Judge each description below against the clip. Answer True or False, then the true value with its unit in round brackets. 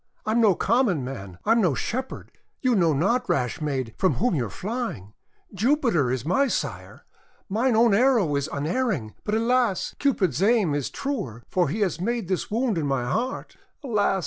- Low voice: False (195 Hz)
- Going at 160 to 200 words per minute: True (185 wpm)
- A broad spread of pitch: True (8.7 semitones)